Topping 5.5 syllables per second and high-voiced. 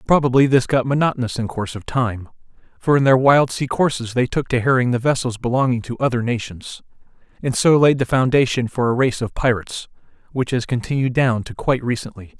No: 5.9 syllables/s; low, 125 Hz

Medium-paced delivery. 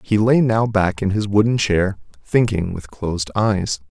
Yes: average, 185 wpm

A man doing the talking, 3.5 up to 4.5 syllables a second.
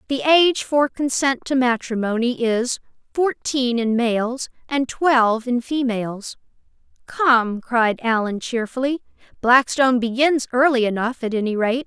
No: female; 4.3 syllables/s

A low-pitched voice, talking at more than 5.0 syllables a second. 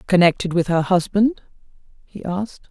No: medium, 185 Hz; 5.3 syllables/s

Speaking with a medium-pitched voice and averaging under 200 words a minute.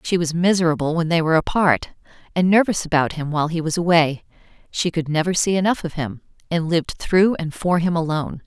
No: medium, 165 Hz; fast, 205 wpm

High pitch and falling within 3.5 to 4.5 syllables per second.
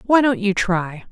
Yes: high, 210 Hz; 4.1 syllables/s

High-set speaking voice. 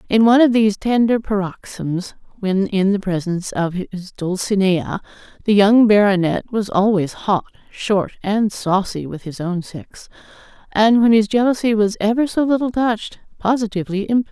Yes: high, 205 Hz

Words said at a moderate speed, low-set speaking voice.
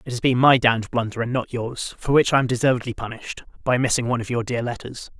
No: fast, 255 wpm; low, 120 Hz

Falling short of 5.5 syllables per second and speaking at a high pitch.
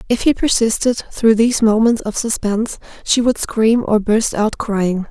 Yes: 4.5 syllables/s; high, 225 Hz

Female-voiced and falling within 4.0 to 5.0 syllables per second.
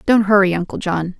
No: female; 5.6 syllables/s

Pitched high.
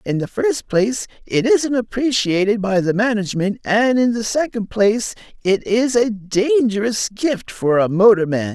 Yes: high, 215 Hz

